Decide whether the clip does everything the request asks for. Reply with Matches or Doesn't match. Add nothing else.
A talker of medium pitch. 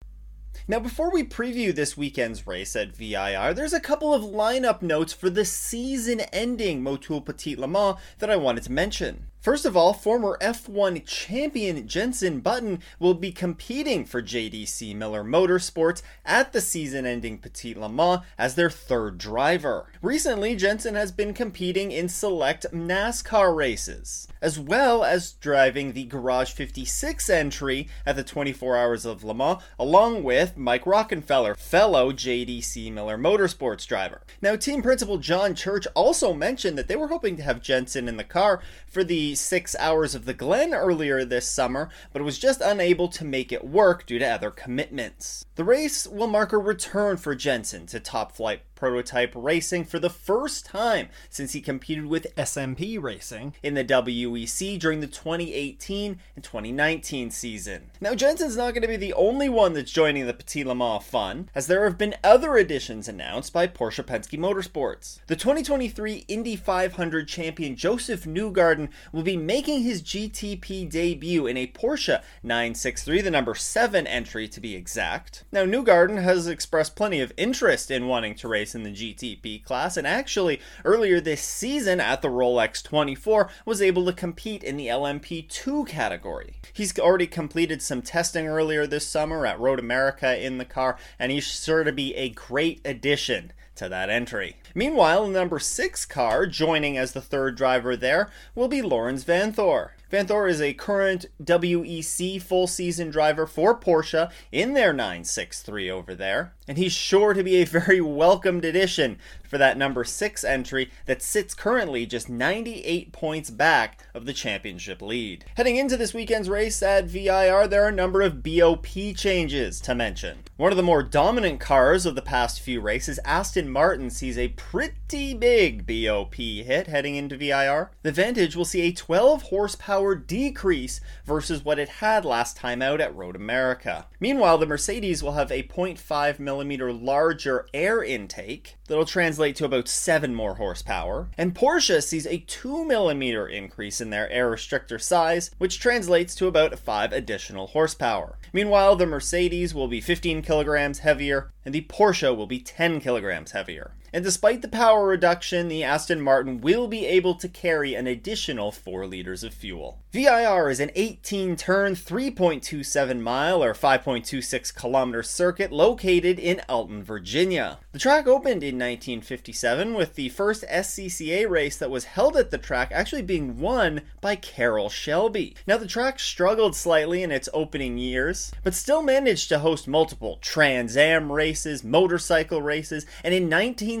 Matches